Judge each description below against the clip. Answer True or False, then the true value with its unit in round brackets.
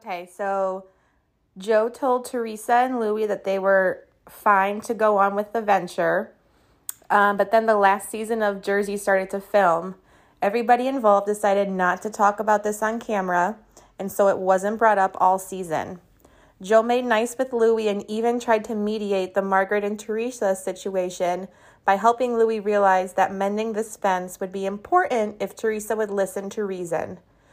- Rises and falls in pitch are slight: True (2.3 semitones)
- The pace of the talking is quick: False (170 wpm)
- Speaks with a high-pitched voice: True (205 Hz)